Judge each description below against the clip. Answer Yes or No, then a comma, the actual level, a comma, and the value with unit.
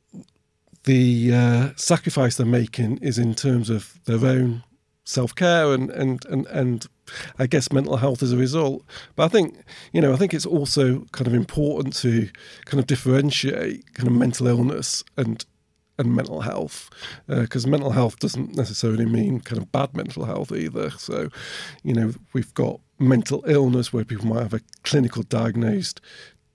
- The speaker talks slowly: No, average, 165 wpm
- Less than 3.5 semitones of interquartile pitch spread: Yes, average, 2.8 semitones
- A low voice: Yes, low, 125 Hz